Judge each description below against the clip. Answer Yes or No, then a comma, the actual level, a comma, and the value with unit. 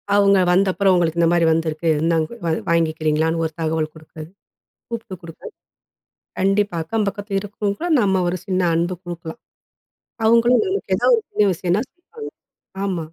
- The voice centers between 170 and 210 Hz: Yes, medium, 185 Hz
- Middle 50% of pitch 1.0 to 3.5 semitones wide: No, average, 3.9 semitones